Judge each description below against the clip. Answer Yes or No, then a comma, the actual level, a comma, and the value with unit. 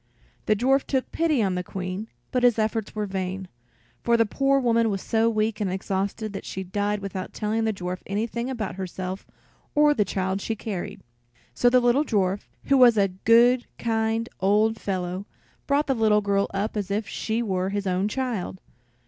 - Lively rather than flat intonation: No, average, 3.2 semitones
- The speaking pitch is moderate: No, high, 215 Hz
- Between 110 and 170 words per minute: No, average, 185 wpm